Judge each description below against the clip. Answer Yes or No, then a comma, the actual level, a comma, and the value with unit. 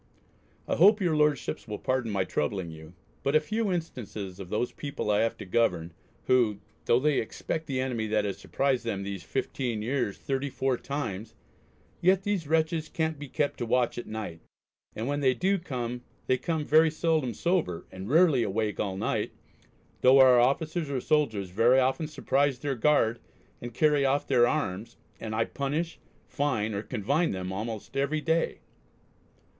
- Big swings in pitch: Yes, wide, 5.9 semitones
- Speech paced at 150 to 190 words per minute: Yes, average, 170 wpm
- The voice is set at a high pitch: No, low, 130 Hz